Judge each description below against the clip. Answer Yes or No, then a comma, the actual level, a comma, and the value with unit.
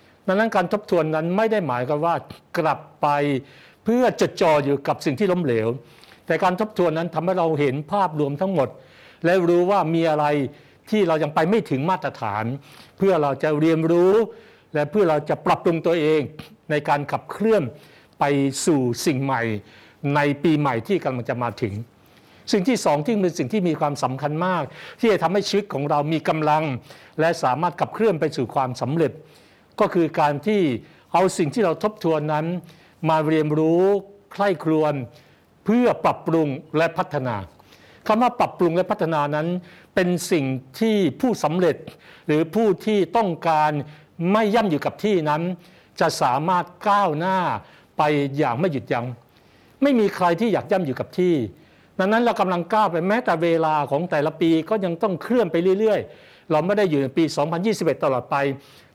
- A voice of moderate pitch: Yes, medium, 160 Hz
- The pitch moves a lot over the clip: No, average, 4.6 semitones